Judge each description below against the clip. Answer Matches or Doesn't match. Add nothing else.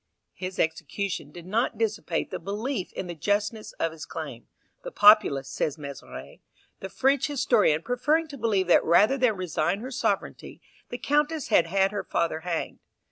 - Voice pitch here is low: Doesn't match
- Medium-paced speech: Matches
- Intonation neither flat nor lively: Doesn't match